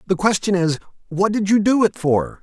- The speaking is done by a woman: No, male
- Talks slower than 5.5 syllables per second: Yes, 5.2 syllables/s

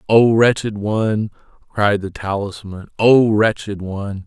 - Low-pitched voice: Yes, low, 105 Hz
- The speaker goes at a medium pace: No, slow, 125 wpm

